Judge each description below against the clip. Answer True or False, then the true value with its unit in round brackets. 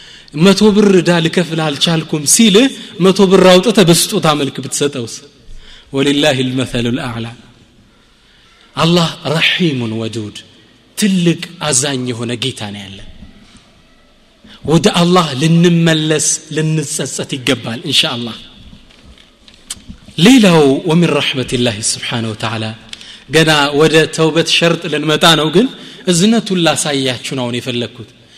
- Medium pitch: True (150 Hz)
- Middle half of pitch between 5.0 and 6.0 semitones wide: True (5.5 semitones)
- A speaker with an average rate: True (95 wpm)